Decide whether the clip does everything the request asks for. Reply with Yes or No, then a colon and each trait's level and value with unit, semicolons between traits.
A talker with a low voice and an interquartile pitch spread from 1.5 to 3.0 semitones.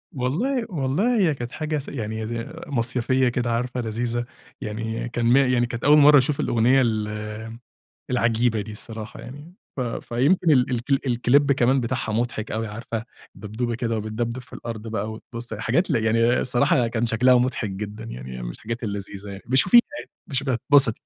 Yes: low, 120 Hz; average, 2.7 semitones